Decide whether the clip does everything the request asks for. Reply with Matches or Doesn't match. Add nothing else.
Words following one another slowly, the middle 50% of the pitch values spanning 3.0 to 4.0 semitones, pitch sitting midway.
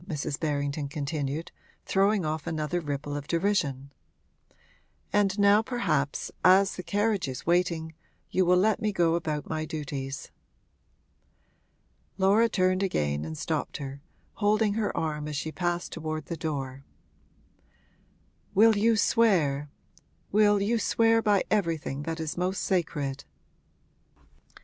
Doesn't match